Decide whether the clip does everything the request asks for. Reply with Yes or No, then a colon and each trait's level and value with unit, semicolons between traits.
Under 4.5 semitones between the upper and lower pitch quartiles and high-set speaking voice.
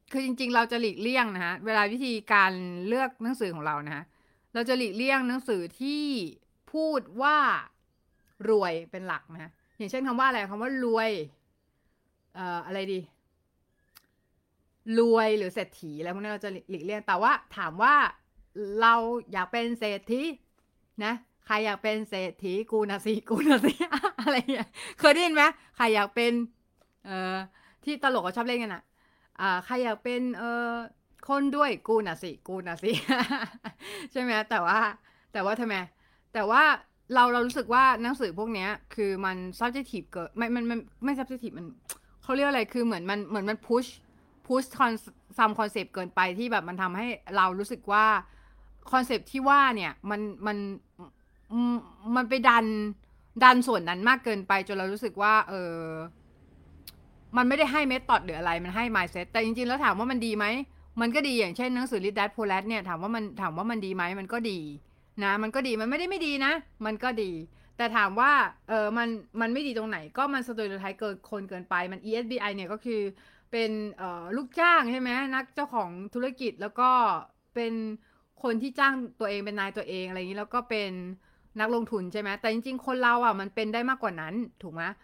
Yes: average, 4.0 semitones; high, 225 Hz